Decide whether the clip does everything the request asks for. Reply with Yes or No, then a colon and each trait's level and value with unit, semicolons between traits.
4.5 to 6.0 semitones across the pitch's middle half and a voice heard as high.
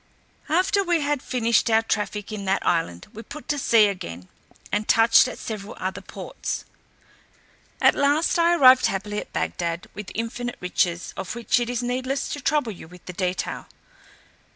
Yes: wide, 5.5 semitones; high, 225 Hz